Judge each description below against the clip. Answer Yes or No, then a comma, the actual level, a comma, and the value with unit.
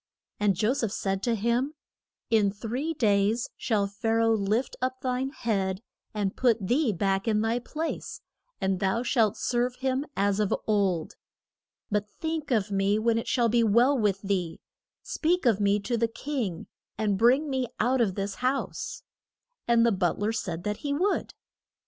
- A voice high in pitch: Yes, high, 225 Hz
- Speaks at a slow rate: No, average, 175 wpm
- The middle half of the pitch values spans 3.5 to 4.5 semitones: Yes, average, 3.8 semitones